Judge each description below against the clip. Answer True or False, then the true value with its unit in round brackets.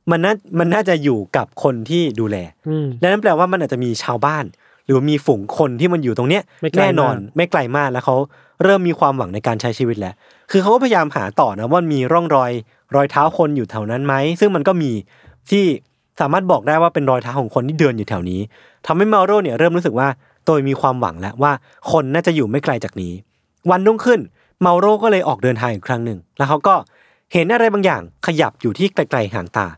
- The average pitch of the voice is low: False (145 Hz)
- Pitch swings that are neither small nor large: False (6.1 semitones)